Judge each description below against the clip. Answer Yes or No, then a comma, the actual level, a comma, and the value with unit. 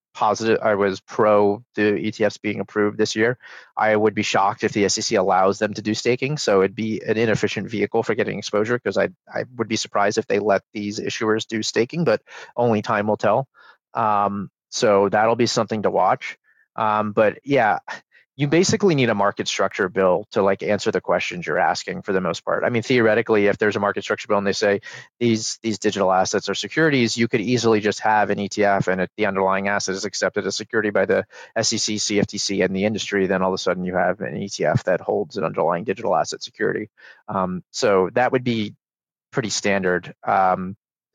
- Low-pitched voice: Yes, low, 105 Hz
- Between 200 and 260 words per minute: Yes, fast, 205 wpm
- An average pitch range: No, narrow, 2.1 semitones